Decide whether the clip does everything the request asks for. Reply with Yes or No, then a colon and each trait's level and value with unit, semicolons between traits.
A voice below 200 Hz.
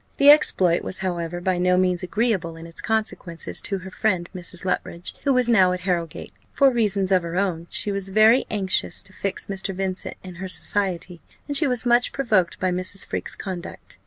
Yes: high, 190 Hz